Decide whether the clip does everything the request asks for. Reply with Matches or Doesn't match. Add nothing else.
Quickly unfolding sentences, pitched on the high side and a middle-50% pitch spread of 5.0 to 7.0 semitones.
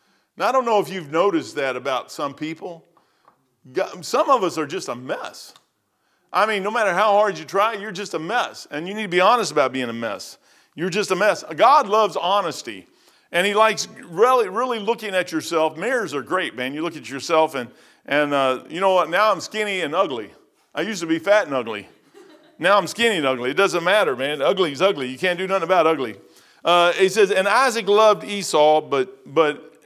Matches